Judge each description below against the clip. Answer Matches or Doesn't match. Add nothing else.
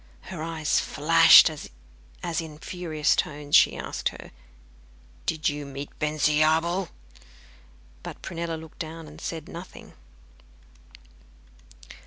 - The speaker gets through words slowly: Matches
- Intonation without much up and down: Matches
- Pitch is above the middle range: Doesn't match